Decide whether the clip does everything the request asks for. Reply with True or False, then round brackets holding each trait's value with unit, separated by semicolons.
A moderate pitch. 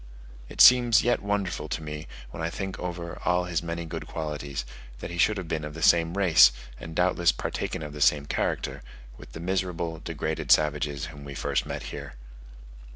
False (80 Hz)